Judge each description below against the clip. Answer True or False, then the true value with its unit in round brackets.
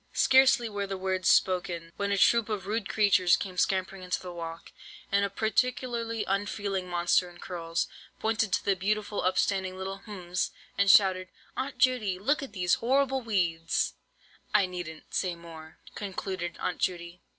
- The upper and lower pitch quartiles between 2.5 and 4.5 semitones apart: True (2.9 semitones)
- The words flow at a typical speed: True (160 wpm)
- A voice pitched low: False (190 Hz)